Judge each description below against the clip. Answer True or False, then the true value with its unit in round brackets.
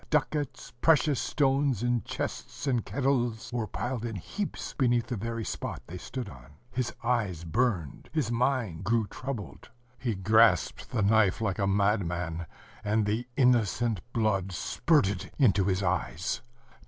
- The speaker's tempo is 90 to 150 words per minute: True (140 wpm)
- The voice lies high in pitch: False (115 Hz)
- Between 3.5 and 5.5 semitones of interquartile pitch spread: True (4.4 semitones)